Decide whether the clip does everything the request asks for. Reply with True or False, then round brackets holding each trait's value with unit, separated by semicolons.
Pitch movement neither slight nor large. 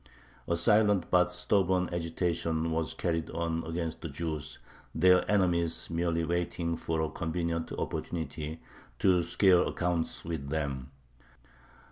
False (1.5 semitones)